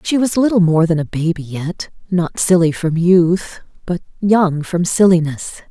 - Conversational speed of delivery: Yes, average, 170 wpm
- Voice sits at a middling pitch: Yes, medium, 175 Hz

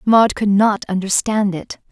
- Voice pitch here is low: No, high, 200 Hz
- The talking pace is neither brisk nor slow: Yes, average, 155 wpm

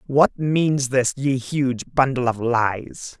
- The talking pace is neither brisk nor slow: Yes, average, 150 wpm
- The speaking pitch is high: No, low, 130 Hz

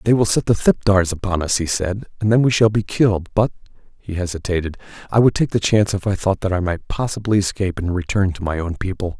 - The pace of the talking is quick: Yes, fast, 235 wpm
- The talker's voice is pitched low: Yes, very low, 95 Hz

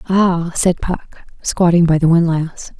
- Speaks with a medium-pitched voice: Yes, medium, 170 Hz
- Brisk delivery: No, average, 150 wpm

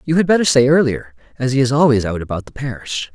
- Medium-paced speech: No, fast, 250 wpm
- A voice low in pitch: Yes, low, 130 Hz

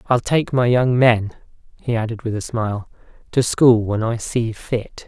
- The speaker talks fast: No, average, 190 wpm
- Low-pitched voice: Yes, low, 115 Hz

